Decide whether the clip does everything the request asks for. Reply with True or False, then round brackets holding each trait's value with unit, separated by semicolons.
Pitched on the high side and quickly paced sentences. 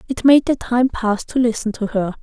True (235 Hz; 240 wpm)